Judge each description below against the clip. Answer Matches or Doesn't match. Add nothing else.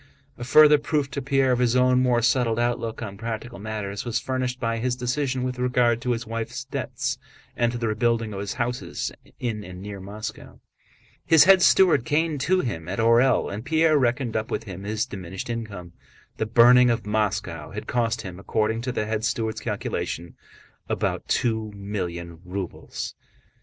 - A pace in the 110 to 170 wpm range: Doesn't match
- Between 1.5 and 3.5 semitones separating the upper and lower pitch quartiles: Matches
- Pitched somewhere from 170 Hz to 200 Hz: Doesn't match